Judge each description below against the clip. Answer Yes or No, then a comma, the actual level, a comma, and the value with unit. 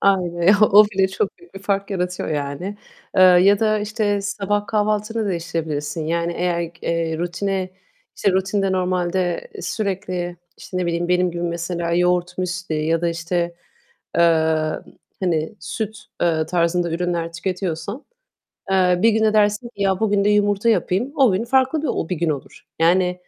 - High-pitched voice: No, medium, 180 Hz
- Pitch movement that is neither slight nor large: Yes, average, 3.0 semitones